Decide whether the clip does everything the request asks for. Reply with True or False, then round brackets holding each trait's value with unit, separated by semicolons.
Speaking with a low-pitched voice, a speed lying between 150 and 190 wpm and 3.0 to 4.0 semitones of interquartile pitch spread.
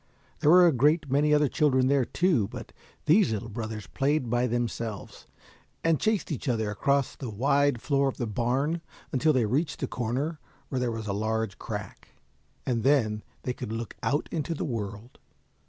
False (130 Hz; 180 wpm; 4.6 semitones)